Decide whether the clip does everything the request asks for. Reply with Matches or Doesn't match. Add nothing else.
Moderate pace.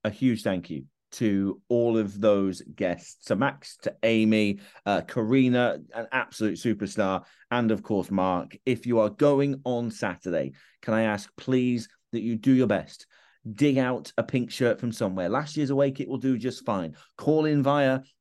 Matches